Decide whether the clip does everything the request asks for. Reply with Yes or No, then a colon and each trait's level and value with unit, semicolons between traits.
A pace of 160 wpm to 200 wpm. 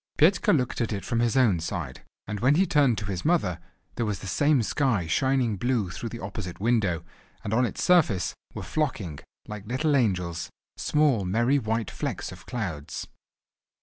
Yes: average, 170 wpm